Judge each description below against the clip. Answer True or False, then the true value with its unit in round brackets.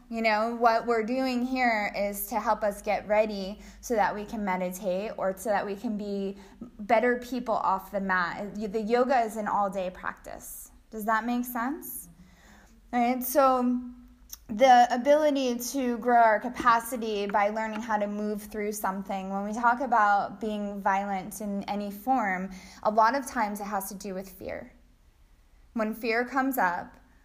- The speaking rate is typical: True (170 wpm)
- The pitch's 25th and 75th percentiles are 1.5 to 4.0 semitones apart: True (3.2 semitones)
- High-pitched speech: True (220 Hz)